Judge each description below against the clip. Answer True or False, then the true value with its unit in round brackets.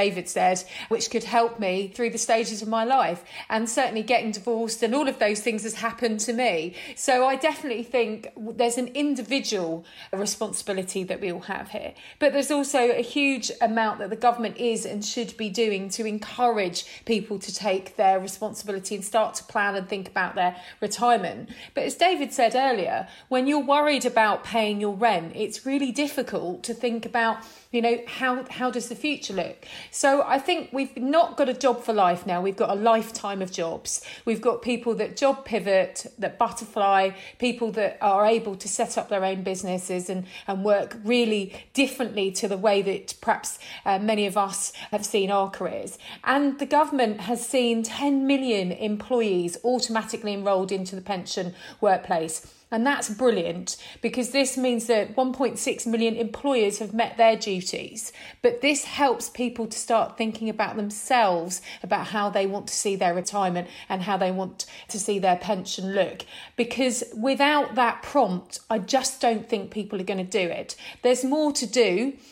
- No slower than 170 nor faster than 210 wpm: True (180 wpm)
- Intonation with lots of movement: False (3.8 semitones)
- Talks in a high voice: True (225 Hz)